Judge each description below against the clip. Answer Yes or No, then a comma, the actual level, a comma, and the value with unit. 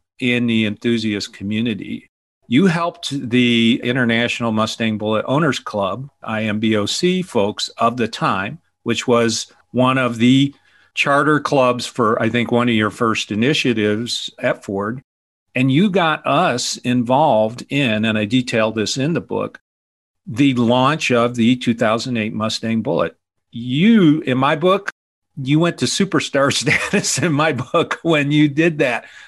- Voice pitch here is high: No, low, 125 Hz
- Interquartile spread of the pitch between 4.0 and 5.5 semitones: Yes, average, 4.7 semitones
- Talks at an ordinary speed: Yes, average, 145 wpm